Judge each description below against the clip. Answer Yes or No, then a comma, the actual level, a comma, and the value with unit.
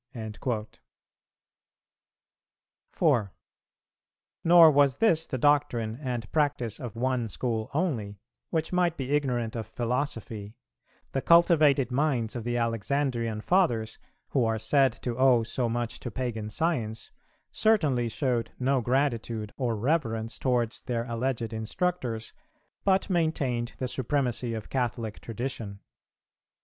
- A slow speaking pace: Yes, slow, 120 wpm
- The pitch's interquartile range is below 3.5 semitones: No, average, 3.9 semitones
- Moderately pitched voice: No, low, 120 Hz